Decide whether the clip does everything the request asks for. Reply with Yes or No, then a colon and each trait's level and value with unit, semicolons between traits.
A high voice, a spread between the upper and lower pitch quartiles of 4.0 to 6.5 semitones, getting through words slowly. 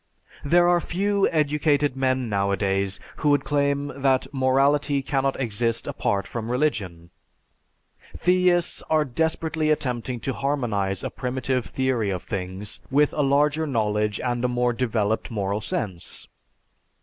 No: low, 130 Hz; average, 5.2 semitones; slow, 130 wpm